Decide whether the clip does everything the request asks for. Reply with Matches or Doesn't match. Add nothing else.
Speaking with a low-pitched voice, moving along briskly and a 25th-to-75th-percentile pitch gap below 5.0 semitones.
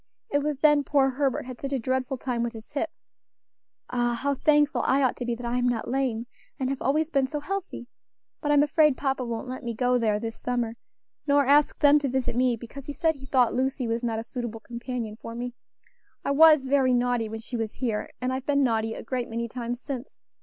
Doesn't match